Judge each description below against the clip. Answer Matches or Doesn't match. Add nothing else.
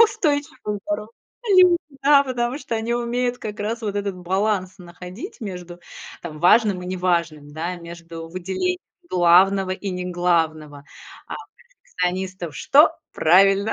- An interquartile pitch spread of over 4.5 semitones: Matches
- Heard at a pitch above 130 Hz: Matches